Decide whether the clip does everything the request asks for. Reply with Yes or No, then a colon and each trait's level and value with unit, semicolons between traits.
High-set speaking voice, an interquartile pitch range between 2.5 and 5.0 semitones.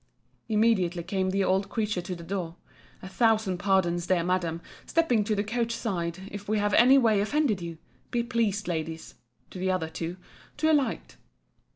Yes: high, 195 Hz; average, 4.2 semitones